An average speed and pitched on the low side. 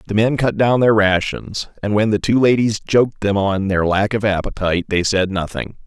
No: fast, 215 wpm; low, 105 Hz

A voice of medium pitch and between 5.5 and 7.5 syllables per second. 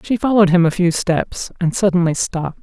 Yes: medium, 180 Hz; 5.7 syllables/s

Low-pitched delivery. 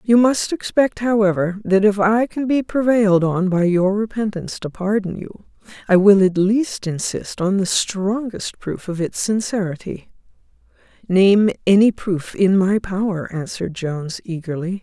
No: high, 200 Hz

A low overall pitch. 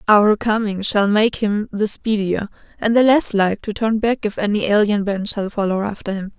No: high, 210 Hz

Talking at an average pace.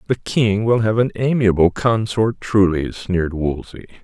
Yes: average, 150 wpm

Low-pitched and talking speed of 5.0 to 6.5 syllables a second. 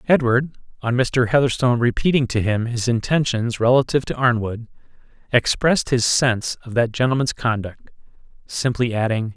Yes: low, 120 Hz; 5.3 syllables/s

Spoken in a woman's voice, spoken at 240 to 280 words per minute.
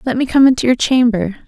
Yes: female; fast, 245 wpm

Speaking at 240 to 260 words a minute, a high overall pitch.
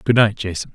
No: fast, 245 wpm; low, 105 Hz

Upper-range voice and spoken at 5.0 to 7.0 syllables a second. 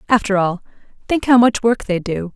Yes: high, 215 Hz; 5.2 syllables/s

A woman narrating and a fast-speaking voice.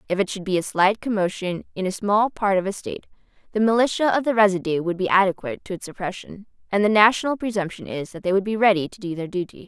Yes: female; fast, 240 wpm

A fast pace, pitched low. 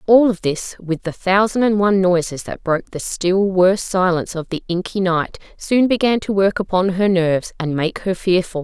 No: fast, 210 wpm; medium, 185 Hz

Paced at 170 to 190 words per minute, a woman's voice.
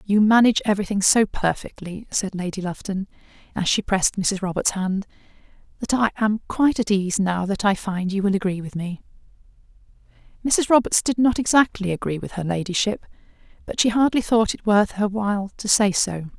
Yes: average, 180 wpm; female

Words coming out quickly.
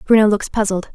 No: average, 190 wpm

